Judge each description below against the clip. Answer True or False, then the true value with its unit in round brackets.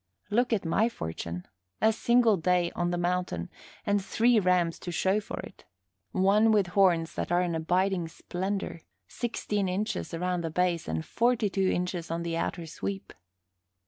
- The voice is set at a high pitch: False (180 Hz)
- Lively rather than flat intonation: False (3.2 semitones)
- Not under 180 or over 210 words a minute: False (165 wpm)